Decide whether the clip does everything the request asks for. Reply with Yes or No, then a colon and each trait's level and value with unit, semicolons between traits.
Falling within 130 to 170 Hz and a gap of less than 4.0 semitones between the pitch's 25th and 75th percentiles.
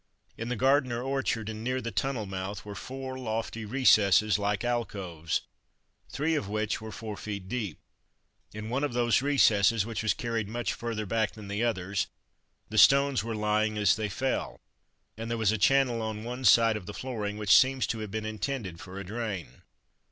No: low, 110 Hz; average, 2.9 semitones